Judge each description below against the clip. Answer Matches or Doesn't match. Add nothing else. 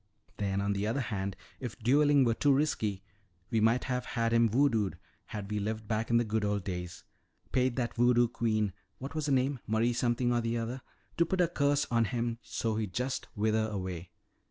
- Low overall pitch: Matches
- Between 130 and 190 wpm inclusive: Doesn't match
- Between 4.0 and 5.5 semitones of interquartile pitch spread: Doesn't match